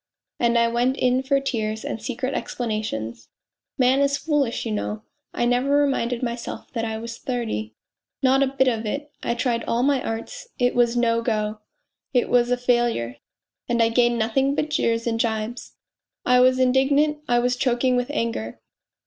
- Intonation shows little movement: Yes, narrow, 2.3 semitones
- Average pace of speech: Yes, average, 180 wpm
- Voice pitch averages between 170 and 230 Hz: No, high, 240 Hz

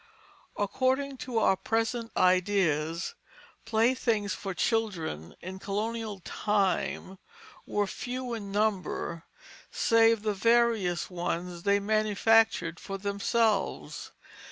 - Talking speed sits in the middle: No, slow, 95 wpm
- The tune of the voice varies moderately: Yes, average, 3.2 semitones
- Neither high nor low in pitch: No, high, 205 Hz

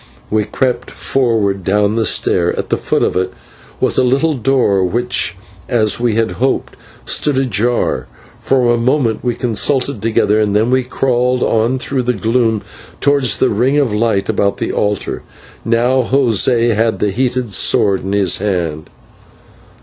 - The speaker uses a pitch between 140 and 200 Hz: No, low, 115 Hz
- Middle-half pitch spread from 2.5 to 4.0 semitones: Yes, average, 3.6 semitones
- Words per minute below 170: Yes, average, 155 wpm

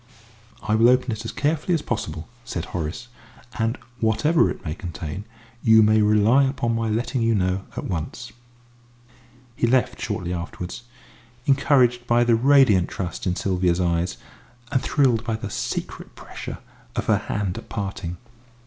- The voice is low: Yes, low, 110 Hz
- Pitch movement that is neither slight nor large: Yes, average, 4.9 semitones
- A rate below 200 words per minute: Yes, average, 155 wpm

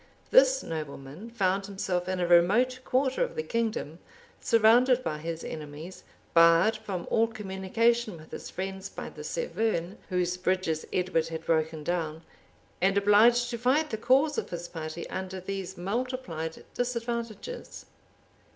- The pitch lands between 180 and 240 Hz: Yes, high, 190 Hz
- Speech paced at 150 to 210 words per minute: No, average, 140 wpm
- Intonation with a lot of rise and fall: Yes, wide, 5.7 semitones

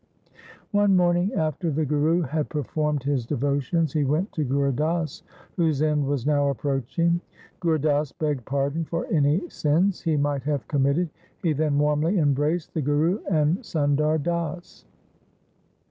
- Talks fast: No, average, 145 wpm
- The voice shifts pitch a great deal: No, average, 2.7 semitones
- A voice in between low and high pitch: Yes, medium, 150 Hz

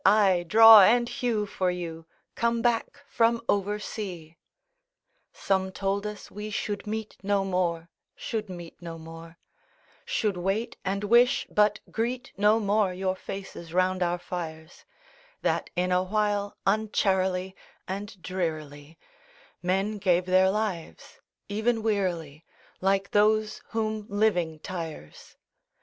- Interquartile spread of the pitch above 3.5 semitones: No, average, 3.0 semitones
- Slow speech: Yes, slow, 125 wpm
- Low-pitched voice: No, high, 195 Hz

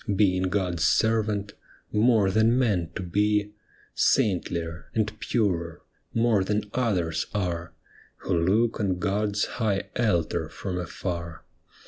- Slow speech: Yes, slow, 115 wpm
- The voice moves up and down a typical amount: Yes, average, 3.2 semitones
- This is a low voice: Yes, low, 100 Hz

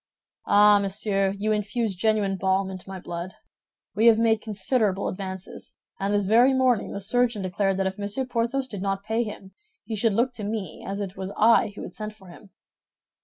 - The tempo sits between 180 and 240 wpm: Yes, average, 195 wpm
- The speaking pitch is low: No, high, 205 Hz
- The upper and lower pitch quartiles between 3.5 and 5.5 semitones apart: No, narrow, 2.6 semitones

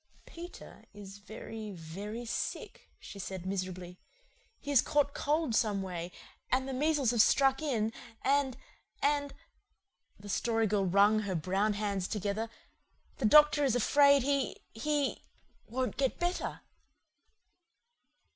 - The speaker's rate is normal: No, slow, 125 wpm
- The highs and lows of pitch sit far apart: Yes, wide, 5.9 semitones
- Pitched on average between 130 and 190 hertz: No, high, 225 Hz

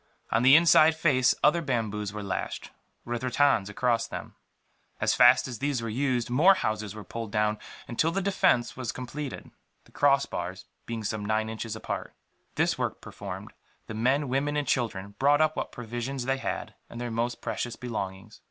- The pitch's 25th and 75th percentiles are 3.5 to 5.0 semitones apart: Yes, average, 4.1 semitones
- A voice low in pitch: Yes, low, 120 Hz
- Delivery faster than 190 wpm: No, average, 175 wpm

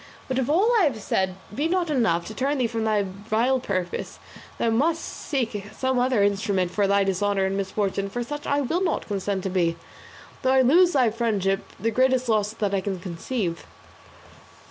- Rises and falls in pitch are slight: No, average, 5.0 semitones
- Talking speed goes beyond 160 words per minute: Yes, average, 190 wpm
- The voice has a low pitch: No, high, 220 Hz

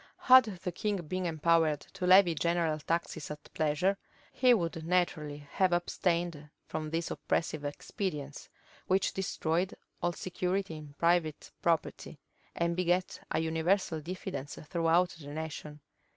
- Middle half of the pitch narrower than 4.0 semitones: Yes, average, 2.7 semitones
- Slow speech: Yes, slow, 130 wpm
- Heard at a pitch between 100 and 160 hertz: No, medium, 170 Hz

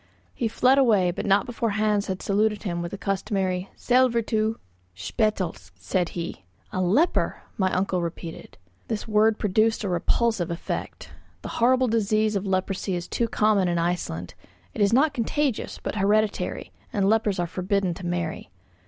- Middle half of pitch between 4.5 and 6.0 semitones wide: No, average, 3.5 semitones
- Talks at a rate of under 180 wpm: Yes, average, 160 wpm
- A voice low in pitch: No, high, 200 Hz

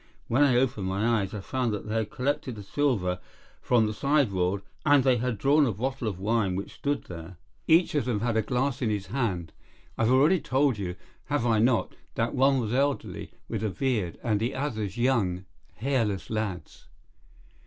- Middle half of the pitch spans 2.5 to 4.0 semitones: No, average, 4.7 semitones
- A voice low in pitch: Yes, low, 115 Hz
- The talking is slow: No, average, 195 wpm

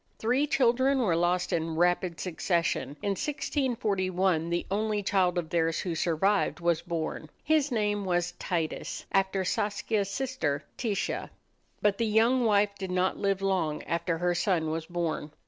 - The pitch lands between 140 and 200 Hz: Yes, medium, 185 Hz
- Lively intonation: No, average, 3.7 semitones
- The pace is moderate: Yes, average, 150 wpm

